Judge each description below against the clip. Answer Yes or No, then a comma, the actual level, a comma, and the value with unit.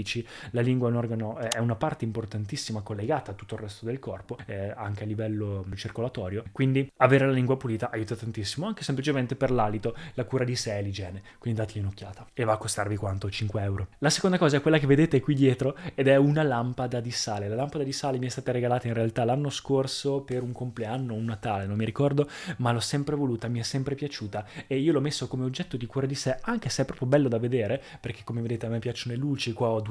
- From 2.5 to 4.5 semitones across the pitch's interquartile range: Yes, average, 3.6 semitones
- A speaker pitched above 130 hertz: No, low, 120 Hz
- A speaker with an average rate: No, fast, 235 wpm